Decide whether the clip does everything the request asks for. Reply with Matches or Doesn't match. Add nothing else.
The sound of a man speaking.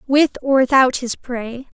Doesn't match